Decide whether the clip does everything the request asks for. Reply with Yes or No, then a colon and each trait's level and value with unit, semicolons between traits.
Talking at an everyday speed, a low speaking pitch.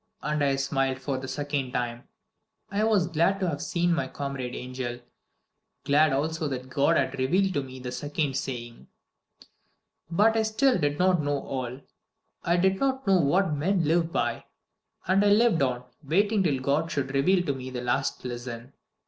No: average, 175 wpm; medium, 145 Hz